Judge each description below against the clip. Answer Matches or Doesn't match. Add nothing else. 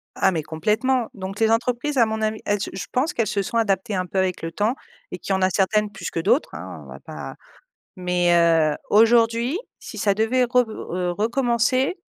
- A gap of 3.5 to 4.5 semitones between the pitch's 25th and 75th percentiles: Matches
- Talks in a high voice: Matches